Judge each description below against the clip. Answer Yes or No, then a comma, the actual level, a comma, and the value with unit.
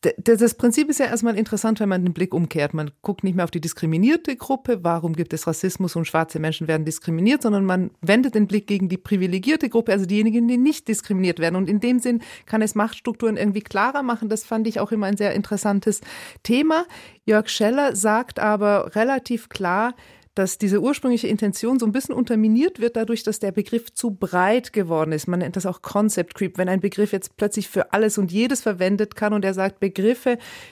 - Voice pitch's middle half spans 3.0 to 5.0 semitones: Yes, average, 3.7 semitones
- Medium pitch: No, high, 210 Hz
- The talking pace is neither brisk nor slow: No, fast, 205 wpm